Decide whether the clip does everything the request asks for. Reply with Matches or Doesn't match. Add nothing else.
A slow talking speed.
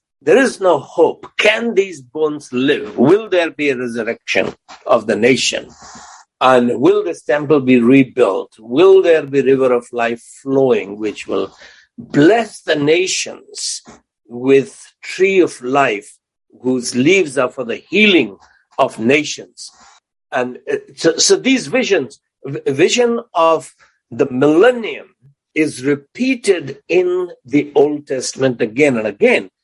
Matches